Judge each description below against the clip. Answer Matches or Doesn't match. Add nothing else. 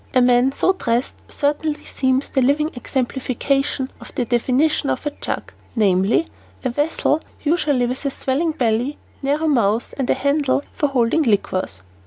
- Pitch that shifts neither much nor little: Matches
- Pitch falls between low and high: Doesn't match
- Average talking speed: Matches